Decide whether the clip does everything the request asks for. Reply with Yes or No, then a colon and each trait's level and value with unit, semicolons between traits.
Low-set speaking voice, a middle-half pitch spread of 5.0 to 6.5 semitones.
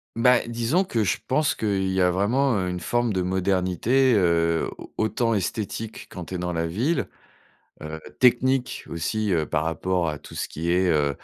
Yes: very low, 95 Hz; wide, 5.4 semitones